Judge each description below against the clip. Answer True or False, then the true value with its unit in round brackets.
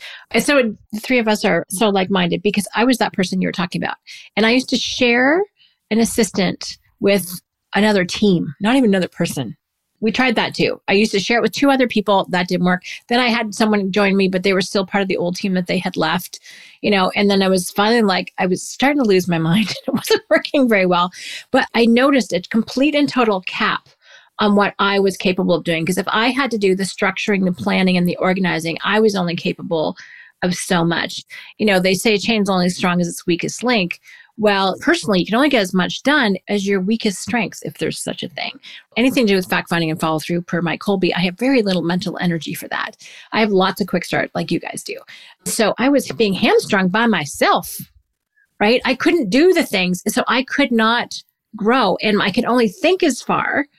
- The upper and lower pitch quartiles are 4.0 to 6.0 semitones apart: True (4.4 semitones)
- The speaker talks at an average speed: False (230 wpm)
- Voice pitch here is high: True (205 Hz)